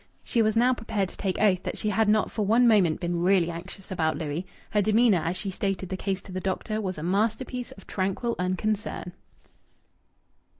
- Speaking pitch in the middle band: No, high, 195 Hz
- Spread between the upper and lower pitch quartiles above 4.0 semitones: No, average, 3.0 semitones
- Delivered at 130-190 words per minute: No, average, 200 wpm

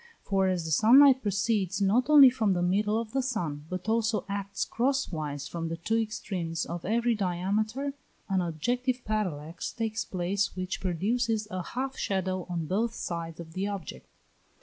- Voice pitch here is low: No, high, 200 Hz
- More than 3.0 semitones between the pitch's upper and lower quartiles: Yes, average, 4.5 semitones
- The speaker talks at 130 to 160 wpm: No, average, 170 wpm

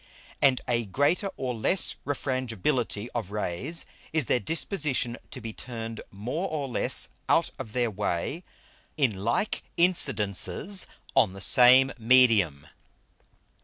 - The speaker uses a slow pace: Yes, slow, 125 wpm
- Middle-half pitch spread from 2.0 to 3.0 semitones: No, average, 5.1 semitones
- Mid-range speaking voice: No, low, 125 Hz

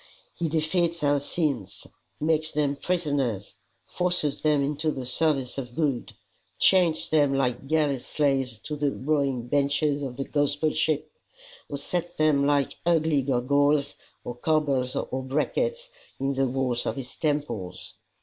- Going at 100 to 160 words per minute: Yes, average, 140 wpm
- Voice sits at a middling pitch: Yes, medium, 145 Hz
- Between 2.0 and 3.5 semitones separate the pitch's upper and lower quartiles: Yes, average, 2.7 semitones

